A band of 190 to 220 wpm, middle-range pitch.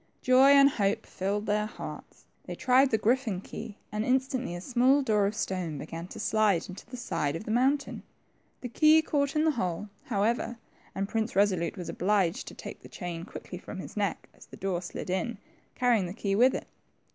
No: average, 200 wpm; high, 215 Hz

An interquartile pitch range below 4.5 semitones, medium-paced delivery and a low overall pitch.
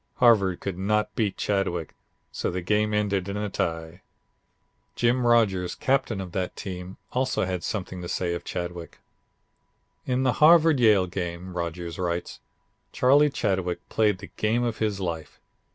Yes: average, 4.0 semitones; average, 150 wpm; very low, 95 Hz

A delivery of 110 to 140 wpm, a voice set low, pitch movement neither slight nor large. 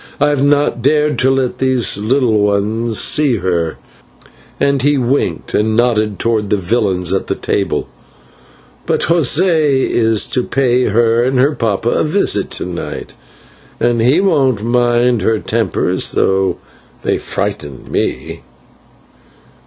Yes: slow, 135 wpm; low, 120 Hz; average, 4.5 semitones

